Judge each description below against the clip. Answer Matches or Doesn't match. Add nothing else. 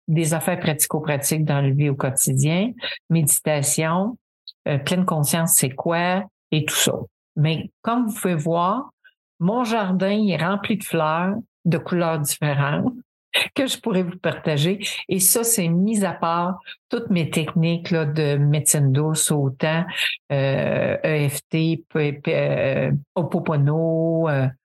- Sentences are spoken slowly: Matches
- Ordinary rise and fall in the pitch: Matches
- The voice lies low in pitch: Doesn't match